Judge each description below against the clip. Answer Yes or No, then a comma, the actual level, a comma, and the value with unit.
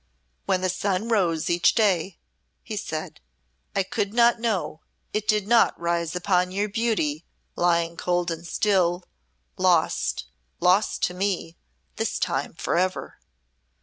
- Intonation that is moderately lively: Yes, average, 3.1 semitones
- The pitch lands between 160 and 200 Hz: Yes, medium, 185 Hz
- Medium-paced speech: No, slow, 130 wpm